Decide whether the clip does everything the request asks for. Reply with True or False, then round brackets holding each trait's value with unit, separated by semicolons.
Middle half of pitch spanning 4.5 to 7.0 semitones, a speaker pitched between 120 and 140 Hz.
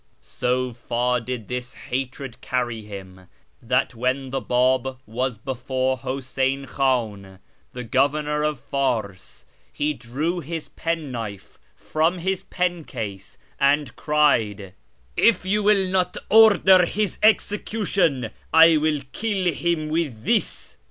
True (5.2 semitones; 135 Hz)